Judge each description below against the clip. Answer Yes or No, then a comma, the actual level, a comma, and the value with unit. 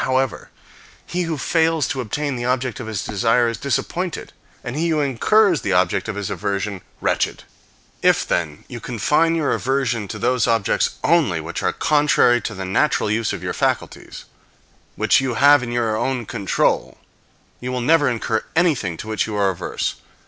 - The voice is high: No, low, 125 Hz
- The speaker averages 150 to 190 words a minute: Yes, average, 180 wpm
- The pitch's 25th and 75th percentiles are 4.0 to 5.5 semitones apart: Yes, average, 5.1 semitones